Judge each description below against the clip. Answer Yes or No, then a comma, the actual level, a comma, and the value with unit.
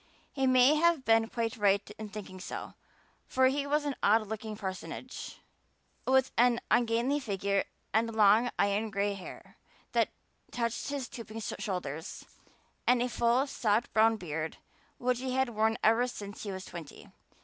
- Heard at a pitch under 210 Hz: No, high, 225 Hz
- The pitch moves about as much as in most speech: Yes, average, 3.7 semitones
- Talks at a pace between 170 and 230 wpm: No, average, 155 wpm